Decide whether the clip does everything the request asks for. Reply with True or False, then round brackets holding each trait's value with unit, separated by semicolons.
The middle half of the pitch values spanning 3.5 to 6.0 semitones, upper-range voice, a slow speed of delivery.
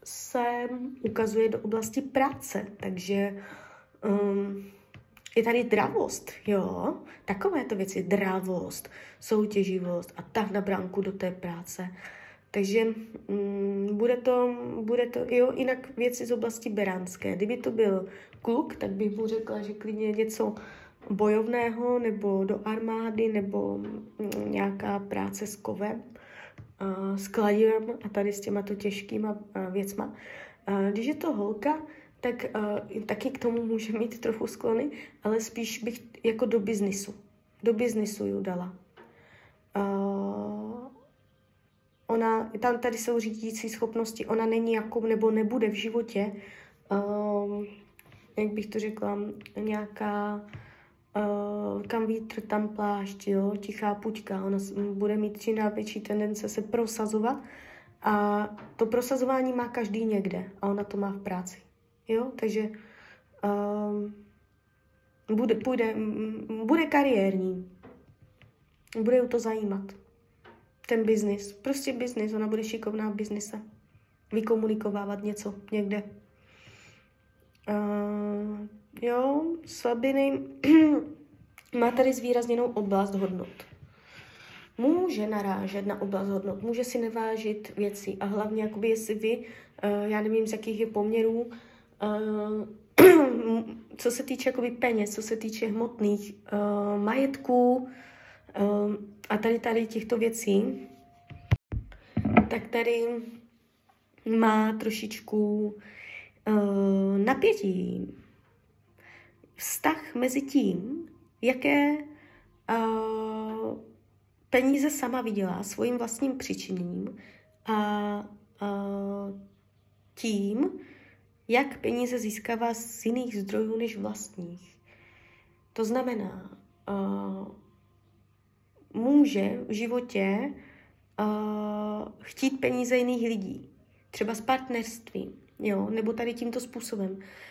False (2.6 semitones; 215 Hz; 110 wpm)